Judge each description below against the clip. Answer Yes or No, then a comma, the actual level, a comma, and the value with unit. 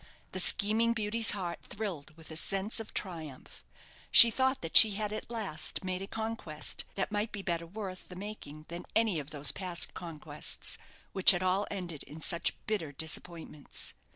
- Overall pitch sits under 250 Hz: Yes, medium, 185 Hz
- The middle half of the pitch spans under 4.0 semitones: No, average, 4.6 semitones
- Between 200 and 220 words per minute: No, average, 175 wpm